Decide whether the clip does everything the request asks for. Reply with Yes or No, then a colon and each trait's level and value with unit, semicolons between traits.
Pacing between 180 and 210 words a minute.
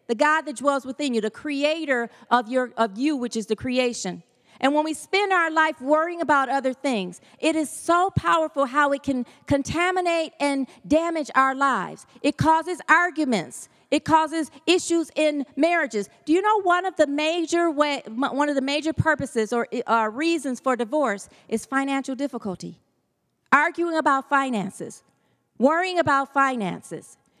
No: average, 160 wpm